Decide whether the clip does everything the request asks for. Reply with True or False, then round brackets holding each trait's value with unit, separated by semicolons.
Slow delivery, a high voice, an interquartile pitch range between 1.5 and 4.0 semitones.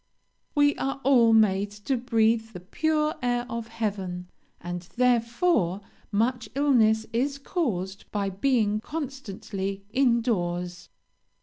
False (115 wpm; 225 Hz; 4.8 semitones)